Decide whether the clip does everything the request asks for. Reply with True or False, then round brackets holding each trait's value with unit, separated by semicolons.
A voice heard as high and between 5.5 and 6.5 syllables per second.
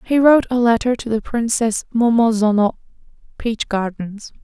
False (230 Hz; 4.9 syllables/s)